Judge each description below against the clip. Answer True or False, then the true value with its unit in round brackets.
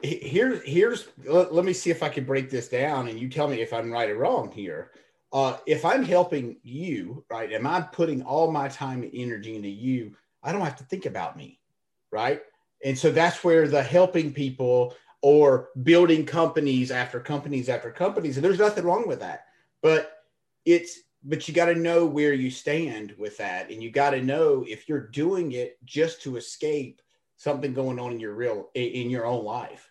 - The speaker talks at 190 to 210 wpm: True (205 wpm)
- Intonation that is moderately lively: True (4.7 semitones)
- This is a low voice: False (145 Hz)